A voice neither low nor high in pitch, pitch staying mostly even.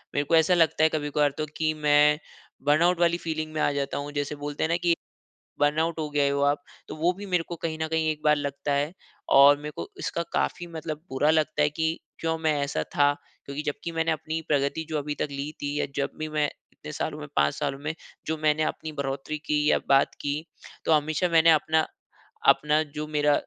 Yes: medium, 150 Hz; narrow, 1.7 semitones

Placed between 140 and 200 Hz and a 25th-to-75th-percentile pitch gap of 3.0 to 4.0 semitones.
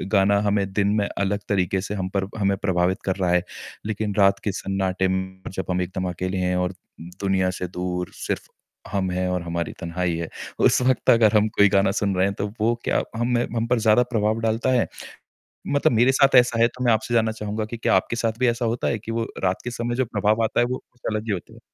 No: low, 105 Hz; average, 3.5 semitones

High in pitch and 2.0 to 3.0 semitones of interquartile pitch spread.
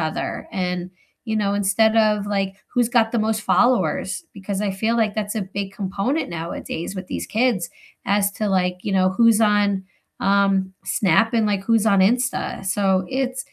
Yes: high, 200 Hz; narrow, 2.6 semitones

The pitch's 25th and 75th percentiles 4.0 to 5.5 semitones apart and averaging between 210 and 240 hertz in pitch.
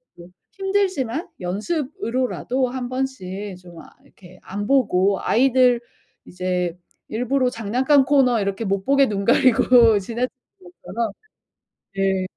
Yes: average, 5.2 semitones; high, 235 Hz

